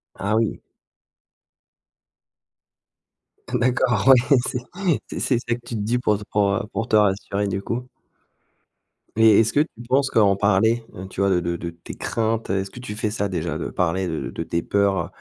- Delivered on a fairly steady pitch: No, average, 3.6 semitones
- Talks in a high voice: No, low, 105 Hz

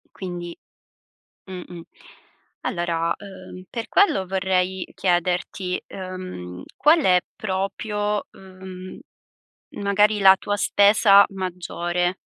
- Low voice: No, medium, 185 Hz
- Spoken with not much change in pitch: Yes, narrow, 1.8 semitones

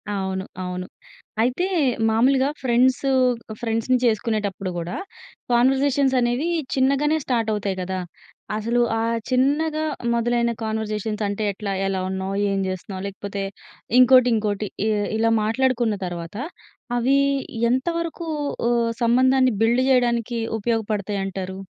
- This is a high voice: Yes, high, 230 Hz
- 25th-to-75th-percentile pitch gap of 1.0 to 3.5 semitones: No, average, 4.2 semitones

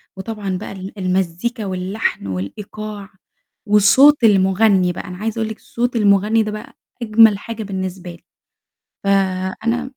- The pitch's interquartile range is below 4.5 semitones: Yes, average, 2.8 semitones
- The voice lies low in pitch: No, high, 200 Hz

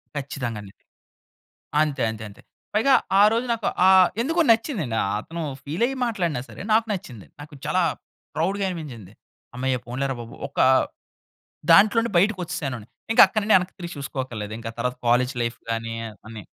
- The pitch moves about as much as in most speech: No, wide, 8.8 semitones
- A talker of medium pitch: Yes, medium, 150 Hz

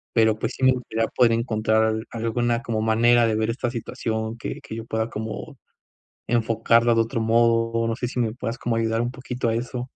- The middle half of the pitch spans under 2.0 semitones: Yes, narrow, 1.2 semitones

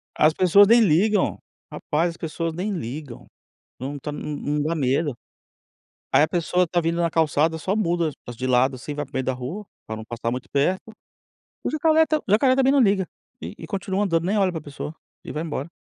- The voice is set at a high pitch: No, medium, 165 Hz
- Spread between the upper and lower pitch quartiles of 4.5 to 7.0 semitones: Yes, average, 5.1 semitones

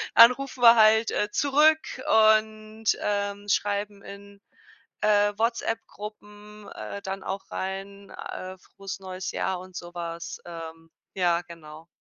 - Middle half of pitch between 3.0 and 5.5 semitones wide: No, narrow, 2.5 semitones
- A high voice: Yes, high, 200 Hz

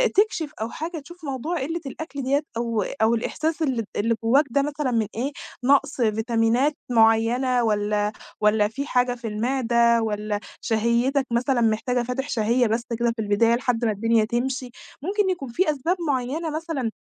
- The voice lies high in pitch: Yes, high, 245 Hz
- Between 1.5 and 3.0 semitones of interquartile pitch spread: No, average, 3.7 semitones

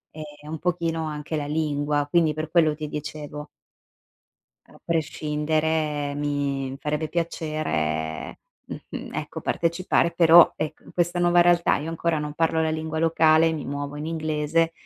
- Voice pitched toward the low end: No, medium, 155 Hz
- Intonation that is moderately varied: No, narrow, 1.8 semitones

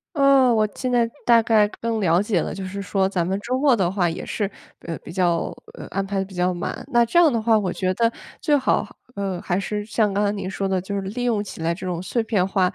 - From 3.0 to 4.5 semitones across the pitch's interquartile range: Yes, average, 3.7 semitones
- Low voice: No, high, 200 Hz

